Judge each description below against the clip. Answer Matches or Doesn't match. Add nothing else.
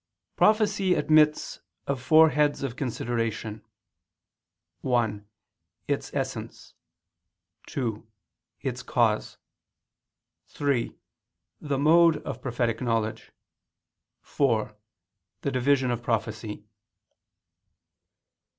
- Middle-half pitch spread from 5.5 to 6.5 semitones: Doesn't match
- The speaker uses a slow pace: Matches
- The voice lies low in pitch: Matches